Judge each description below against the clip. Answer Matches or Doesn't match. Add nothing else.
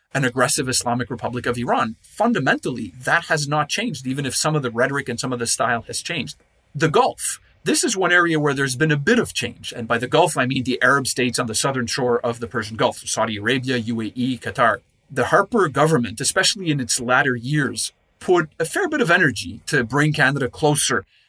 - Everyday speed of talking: Doesn't match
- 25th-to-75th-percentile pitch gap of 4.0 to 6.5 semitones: Doesn't match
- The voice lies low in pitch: Matches